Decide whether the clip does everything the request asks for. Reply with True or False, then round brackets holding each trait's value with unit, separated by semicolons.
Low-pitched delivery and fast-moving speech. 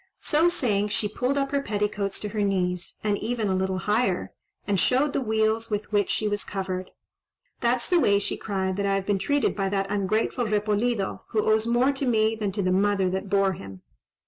False (210 Hz; 210 wpm)